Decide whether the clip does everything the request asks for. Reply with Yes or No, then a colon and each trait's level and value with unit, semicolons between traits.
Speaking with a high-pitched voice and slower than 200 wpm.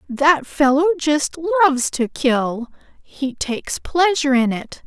Yes: very high, 290 Hz; slow, 135 wpm